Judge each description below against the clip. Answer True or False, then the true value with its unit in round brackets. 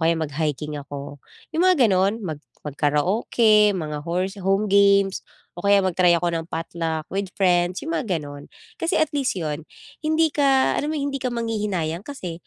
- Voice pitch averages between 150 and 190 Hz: True (185 Hz)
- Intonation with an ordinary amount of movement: False (5.9 semitones)